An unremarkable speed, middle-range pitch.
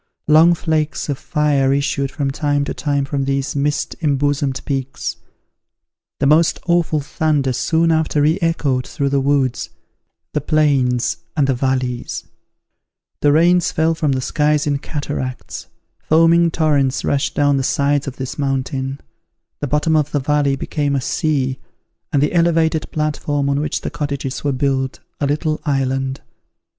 Yes: average, 150 wpm; medium, 145 Hz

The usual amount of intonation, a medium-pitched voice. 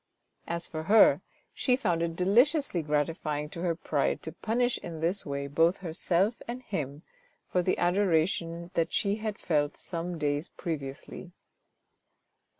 Yes: average, 3.9 semitones; medium, 170 Hz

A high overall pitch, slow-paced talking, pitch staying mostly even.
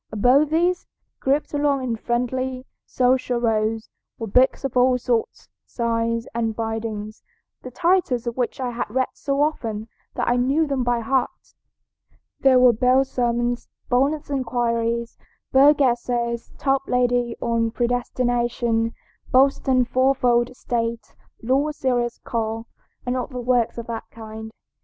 Yes: high, 245 Hz; slow, 130 wpm; narrow, 2.1 semitones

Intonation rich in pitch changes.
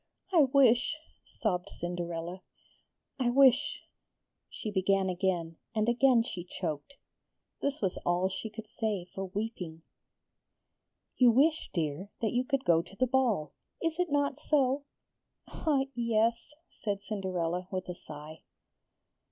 Yes: wide, 6.3 semitones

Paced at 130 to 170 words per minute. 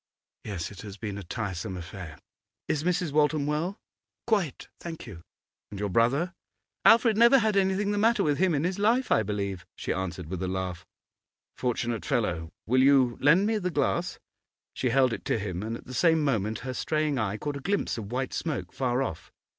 No: average, 195 wpm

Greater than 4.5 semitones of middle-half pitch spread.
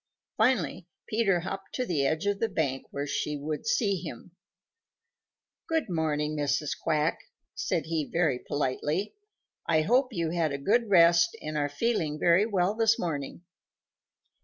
Yes: average, 5.2 semitones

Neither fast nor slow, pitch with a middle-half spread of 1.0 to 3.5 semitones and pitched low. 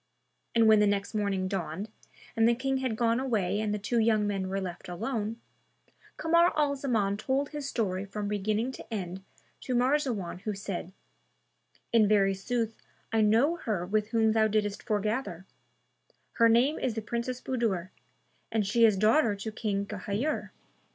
No: average, 165 wpm; average, 3.0 semitones; high, 215 Hz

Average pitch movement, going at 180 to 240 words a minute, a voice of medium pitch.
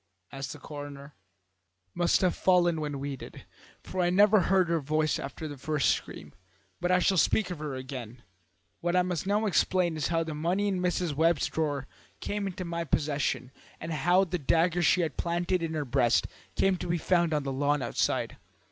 Yes: average, 3.8 semitones; average, 195 wpm; medium, 165 Hz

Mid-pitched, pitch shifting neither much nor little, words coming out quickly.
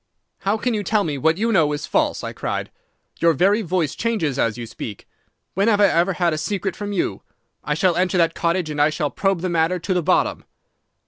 Yes: medium, 175 Hz; average, 4.2 semitones; fast, 230 wpm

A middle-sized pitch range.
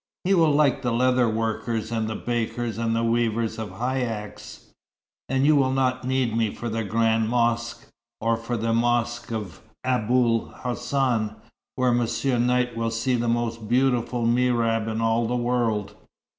No: narrow, 1.7 semitones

